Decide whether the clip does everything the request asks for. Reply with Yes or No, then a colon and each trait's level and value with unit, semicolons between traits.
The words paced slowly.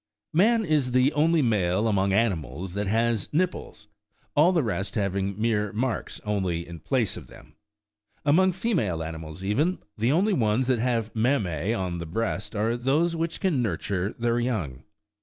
No: average, 160 wpm